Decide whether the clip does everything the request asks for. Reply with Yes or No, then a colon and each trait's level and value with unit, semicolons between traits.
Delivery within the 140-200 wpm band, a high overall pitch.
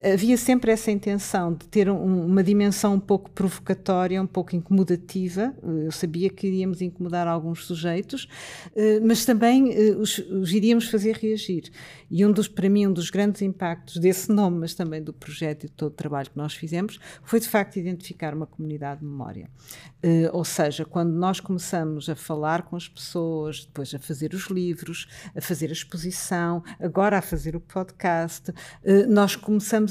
No: average, 170 wpm; medium, 180 Hz